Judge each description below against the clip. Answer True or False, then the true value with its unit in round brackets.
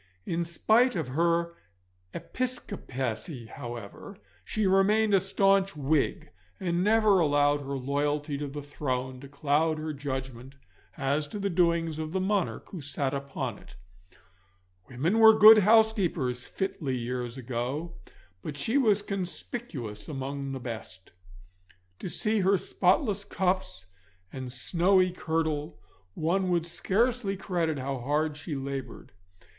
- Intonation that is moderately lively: False (6.1 semitones)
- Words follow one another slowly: True (130 wpm)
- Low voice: False (155 Hz)